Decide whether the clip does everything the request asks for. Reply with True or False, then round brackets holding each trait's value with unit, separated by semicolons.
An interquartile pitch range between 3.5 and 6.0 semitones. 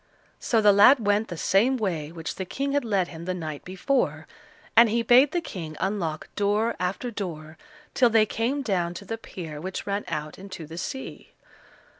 True (5.2 semitones)